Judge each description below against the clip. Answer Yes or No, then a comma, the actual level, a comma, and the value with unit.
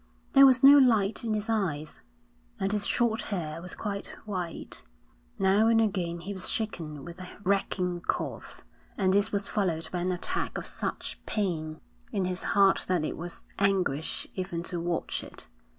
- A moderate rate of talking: Yes, average, 170 wpm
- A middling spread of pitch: Yes, average, 3.4 semitones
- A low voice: No, high, 190 Hz